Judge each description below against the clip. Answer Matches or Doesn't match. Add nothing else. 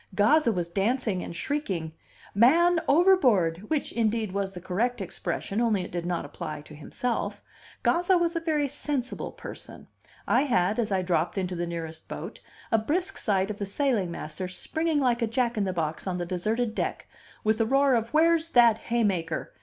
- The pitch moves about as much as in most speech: Doesn't match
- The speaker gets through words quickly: Doesn't match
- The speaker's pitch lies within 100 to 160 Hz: Doesn't match